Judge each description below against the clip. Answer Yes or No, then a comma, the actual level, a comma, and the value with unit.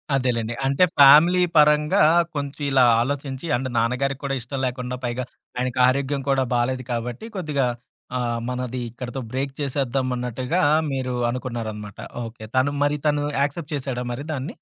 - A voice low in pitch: Yes, low, 130 Hz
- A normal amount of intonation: No, narrow, 2.3 semitones